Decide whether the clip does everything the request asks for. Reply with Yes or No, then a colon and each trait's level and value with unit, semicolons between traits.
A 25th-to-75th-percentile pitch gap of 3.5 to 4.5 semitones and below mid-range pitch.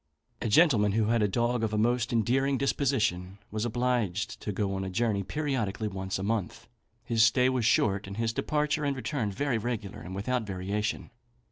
Yes: average, 3.8 semitones; low, 110 Hz